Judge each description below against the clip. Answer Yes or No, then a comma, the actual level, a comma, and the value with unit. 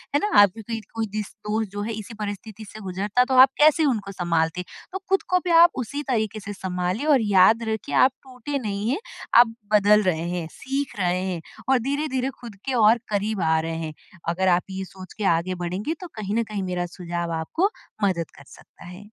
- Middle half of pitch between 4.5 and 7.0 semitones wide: Yes, average, 4.8 semitones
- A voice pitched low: No, high, 205 Hz